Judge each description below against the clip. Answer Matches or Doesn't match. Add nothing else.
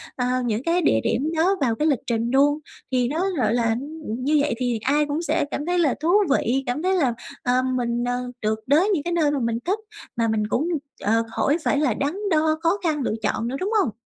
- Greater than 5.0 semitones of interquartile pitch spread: Doesn't match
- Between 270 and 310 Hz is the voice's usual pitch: Matches